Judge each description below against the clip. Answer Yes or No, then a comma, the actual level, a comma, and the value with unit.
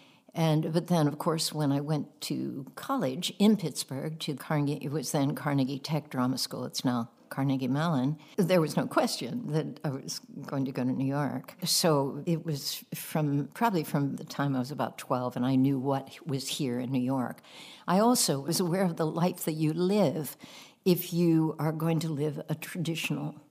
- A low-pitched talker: No, medium, 155 Hz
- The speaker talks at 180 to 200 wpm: Yes, average, 195 wpm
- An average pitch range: Yes, average, 3.5 semitones